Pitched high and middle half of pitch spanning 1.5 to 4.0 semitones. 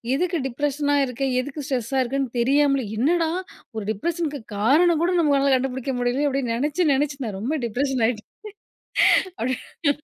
Yes: very high, 275 Hz; average, 2.9 semitones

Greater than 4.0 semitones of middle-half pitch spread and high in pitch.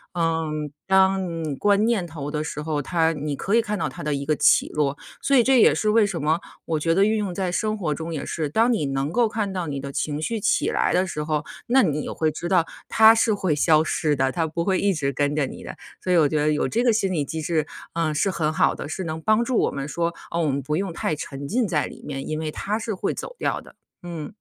No: average, 4.7 semitones; medium, 165 Hz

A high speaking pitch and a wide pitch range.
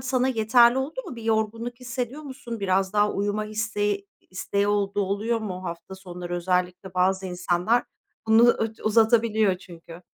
No: high, 210 Hz; average, 3.6 semitones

